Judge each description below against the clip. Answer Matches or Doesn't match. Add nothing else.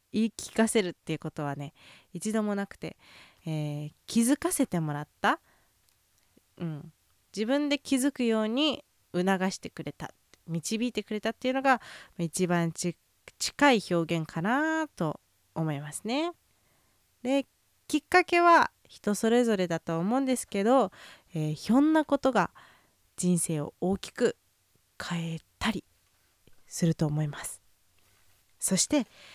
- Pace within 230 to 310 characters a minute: Matches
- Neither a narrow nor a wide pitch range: Doesn't match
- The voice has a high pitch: Matches